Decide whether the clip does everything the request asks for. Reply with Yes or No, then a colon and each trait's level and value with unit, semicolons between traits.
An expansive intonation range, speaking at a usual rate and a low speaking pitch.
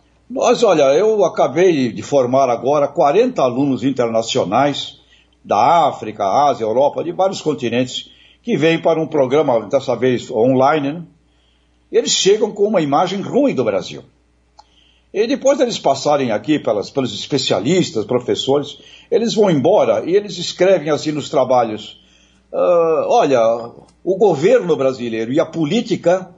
No: wide, 7.2 semitones; average, 140 wpm; medium, 145 Hz